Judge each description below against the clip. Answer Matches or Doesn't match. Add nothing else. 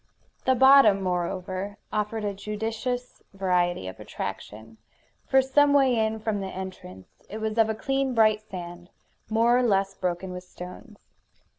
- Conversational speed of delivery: Matches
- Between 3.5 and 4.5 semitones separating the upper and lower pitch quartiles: Matches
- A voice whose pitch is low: Doesn't match